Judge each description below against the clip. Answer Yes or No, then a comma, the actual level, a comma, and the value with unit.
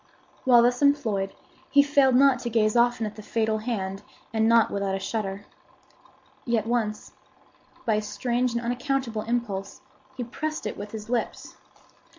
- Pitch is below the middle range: No, high, 230 Hz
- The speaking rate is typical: Yes, average, 160 wpm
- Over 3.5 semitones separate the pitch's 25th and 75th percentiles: No, narrow, 2.6 semitones